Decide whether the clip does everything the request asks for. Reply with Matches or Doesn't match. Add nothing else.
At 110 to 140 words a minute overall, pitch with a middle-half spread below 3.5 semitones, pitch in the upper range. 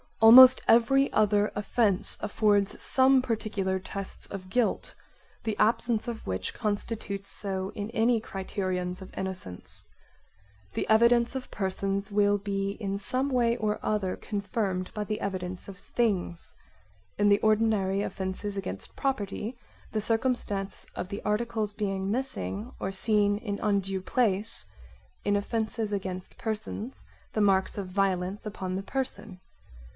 Matches